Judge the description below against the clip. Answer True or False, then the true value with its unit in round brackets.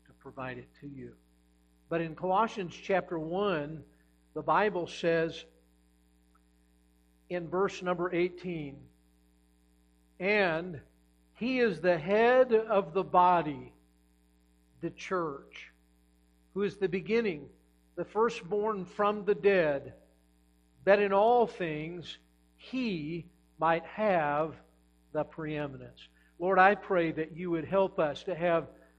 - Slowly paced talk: True (110 wpm)